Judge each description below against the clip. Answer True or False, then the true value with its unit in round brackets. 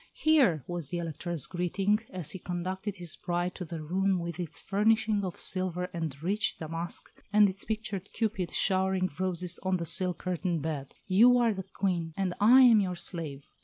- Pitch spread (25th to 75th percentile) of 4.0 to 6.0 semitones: False (2.6 semitones)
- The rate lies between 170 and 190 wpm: True (180 wpm)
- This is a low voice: False (185 Hz)